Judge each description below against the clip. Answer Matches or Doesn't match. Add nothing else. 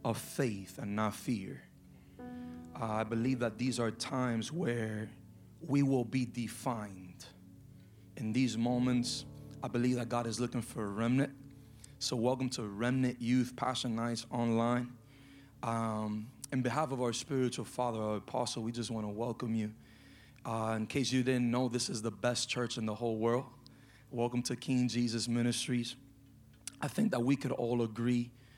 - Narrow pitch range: Matches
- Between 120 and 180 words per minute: Matches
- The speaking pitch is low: Matches